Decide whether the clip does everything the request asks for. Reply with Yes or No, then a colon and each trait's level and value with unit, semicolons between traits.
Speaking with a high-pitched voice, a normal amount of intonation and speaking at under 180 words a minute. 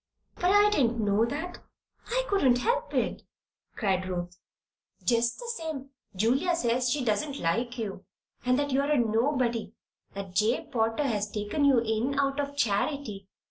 Yes: high, 245 Hz; average, 4.9 semitones; average, 155 wpm